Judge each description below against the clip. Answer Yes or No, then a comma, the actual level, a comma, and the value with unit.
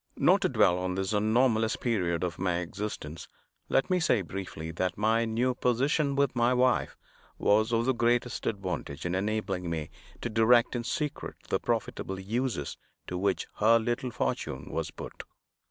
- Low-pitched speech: Yes, low, 110 Hz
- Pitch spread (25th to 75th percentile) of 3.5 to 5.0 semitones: Yes, average, 4.7 semitones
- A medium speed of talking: Yes, average, 165 wpm